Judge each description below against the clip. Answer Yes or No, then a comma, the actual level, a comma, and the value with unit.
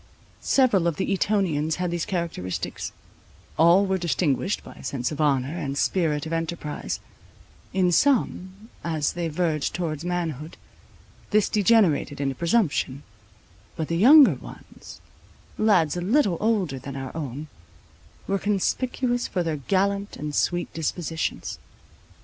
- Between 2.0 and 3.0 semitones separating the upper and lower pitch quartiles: No, average, 4.5 semitones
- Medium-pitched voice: Yes, medium, 170 Hz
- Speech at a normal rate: No, slow, 130 wpm